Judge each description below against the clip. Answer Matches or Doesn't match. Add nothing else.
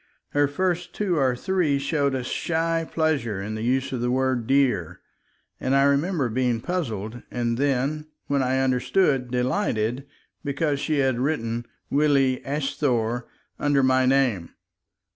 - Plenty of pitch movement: Doesn't match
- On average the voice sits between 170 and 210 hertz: Doesn't match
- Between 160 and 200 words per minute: Doesn't match